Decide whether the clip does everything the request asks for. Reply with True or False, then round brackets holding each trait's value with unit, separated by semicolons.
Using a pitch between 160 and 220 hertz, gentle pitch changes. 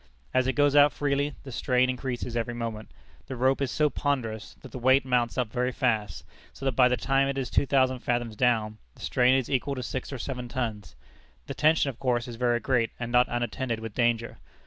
False (125 Hz; 2.1 semitones)